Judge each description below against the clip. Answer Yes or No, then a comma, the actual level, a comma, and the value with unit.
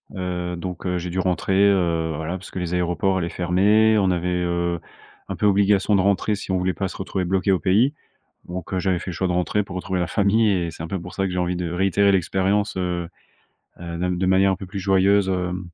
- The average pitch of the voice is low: Yes, very low, 95 Hz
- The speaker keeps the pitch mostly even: Yes, narrow, 1.7 semitones